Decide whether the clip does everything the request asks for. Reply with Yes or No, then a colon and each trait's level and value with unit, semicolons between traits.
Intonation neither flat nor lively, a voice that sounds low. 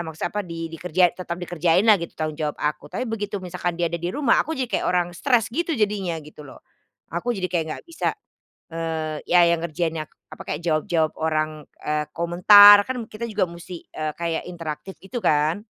No: average, 4.1 semitones; medium, 175 Hz